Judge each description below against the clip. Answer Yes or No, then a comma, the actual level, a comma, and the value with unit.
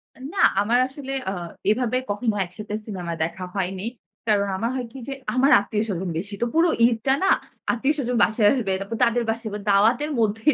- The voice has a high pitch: Yes, high, 225 Hz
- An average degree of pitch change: Yes, average, 3.9 semitones